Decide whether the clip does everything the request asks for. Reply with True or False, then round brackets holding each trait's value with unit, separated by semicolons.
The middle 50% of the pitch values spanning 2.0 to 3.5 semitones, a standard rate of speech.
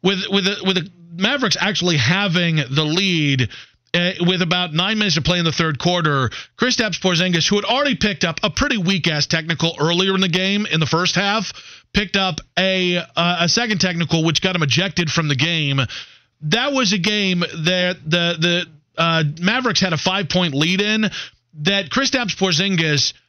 True (3.2 semitones; 185 wpm)